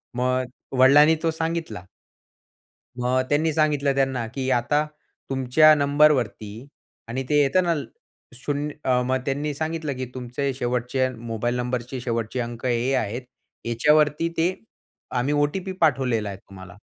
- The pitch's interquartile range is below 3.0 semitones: No, average, 3.4 semitones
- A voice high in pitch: No, low, 130 Hz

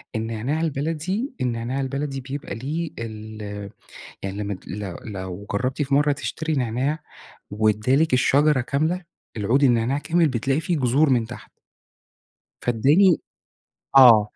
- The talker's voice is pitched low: Yes, low, 130 Hz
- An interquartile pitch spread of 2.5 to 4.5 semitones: No, average, 5.1 semitones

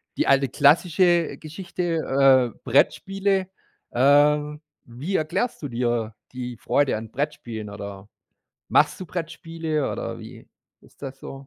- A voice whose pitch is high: No, medium, 145 Hz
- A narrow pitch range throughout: No, average, 5.1 semitones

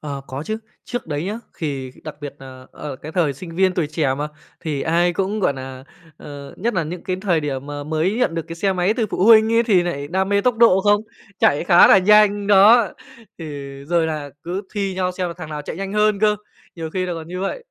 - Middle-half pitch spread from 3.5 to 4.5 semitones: No, average, 5.1 semitones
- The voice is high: No, medium, 175 Hz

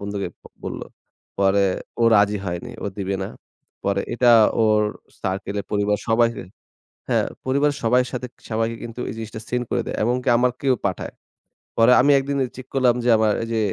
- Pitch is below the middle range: Yes, low, 115 Hz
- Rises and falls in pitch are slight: No, average, 3.5 semitones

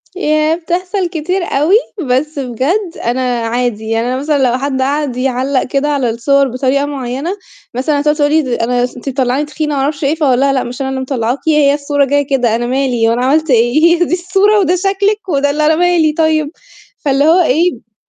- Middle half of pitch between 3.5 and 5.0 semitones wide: Yes, average, 3.8 semitones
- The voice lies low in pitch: No, very high, 280 Hz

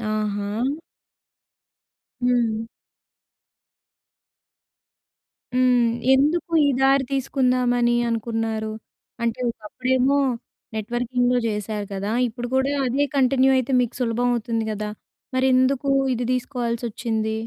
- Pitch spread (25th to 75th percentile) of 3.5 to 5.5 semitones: No, narrow, 2.5 semitones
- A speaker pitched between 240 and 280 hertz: Yes, high, 245 Hz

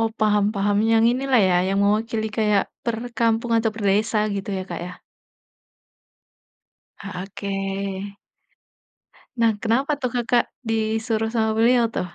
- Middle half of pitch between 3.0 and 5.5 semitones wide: No, narrow, 2.4 semitones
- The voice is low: No, high, 220 Hz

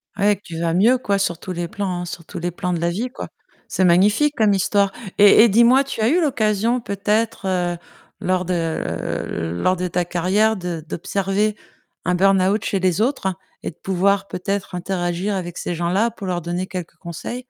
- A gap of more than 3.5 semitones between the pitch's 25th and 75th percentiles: No, average, 3.1 semitones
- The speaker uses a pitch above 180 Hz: Yes, high, 190 Hz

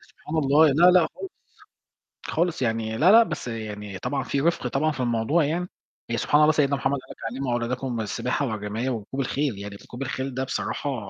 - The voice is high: No, low, 135 Hz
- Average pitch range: Yes, average, 4.6 semitones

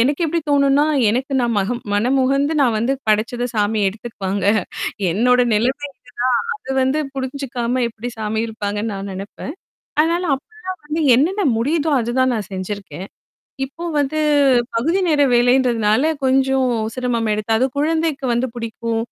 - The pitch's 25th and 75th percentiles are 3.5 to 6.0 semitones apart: Yes, average, 4.2 semitones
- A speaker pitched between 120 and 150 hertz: No, very high, 250 Hz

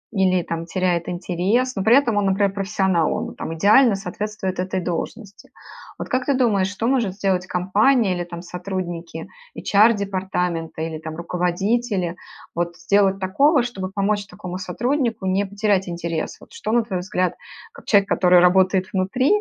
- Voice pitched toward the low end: No, high, 190 Hz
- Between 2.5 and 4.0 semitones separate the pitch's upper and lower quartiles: Yes, average, 2.9 semitones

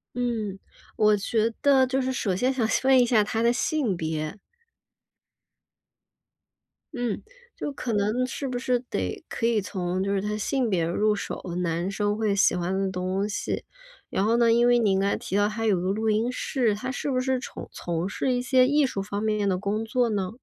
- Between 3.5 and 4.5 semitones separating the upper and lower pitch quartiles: Yes, average, 4.0 semitones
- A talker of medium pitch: No, high, 215 Hz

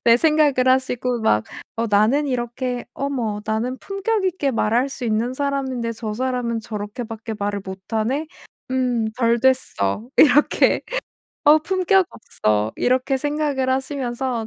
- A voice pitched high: Yes, very high, 250 Hz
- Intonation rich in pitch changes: No, average, 3.7 semitones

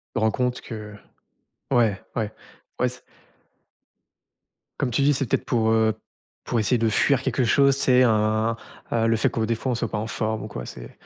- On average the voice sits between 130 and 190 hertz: No, low, 115 Hz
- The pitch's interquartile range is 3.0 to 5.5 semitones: No, narrow, 2.4 semitones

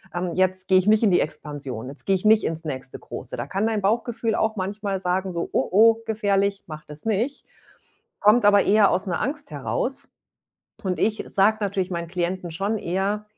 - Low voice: No, high, 195 Hz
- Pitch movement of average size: Yes, average, 3.2 semitones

